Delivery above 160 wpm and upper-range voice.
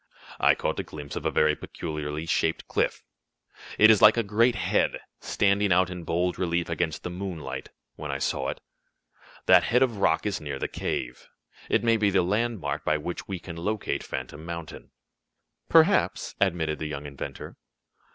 No: average, 175 wpm; very low, 85 Hz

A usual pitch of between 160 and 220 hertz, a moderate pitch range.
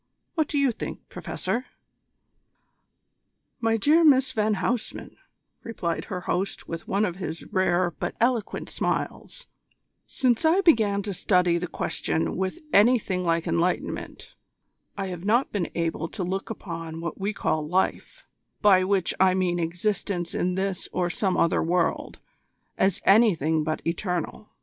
Yes: high, 190 Hz; average, 4.2 semitones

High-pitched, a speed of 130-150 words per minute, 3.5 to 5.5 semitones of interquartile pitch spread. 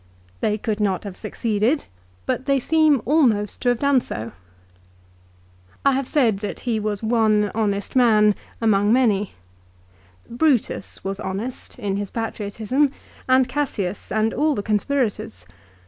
Yes: high, 220 Hz; slow, 135 wpm; average, 4.0 semitones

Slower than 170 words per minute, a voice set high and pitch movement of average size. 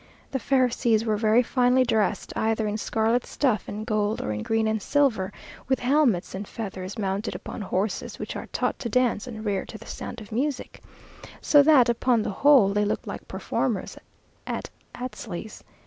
No: average, 180 wpm; high, 225 Hz; average, 3.2 semitones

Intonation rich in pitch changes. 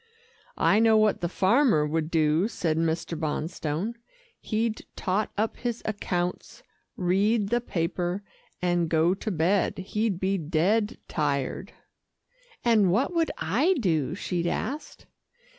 No: average, 4.8 semitones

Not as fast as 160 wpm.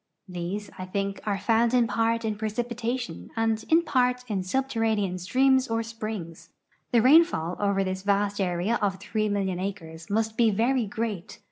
No: average, 165 wpm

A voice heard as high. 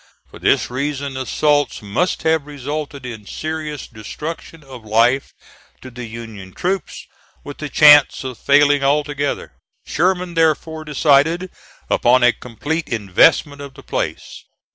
No: medium, 145 Hz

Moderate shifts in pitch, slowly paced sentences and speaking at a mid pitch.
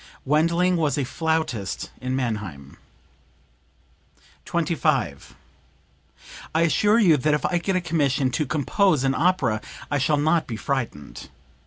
Yes: average, 4.6 semitones; slow, 130 wpm; medium, 150 Hz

